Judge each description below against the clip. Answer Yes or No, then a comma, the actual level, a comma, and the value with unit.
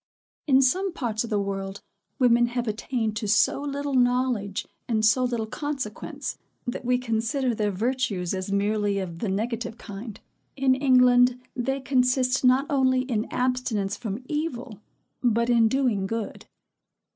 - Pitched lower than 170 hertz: No, high, 240 Hz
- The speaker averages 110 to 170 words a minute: Yes, average, 145 wpm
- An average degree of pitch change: Yes, average, 3.3 semitones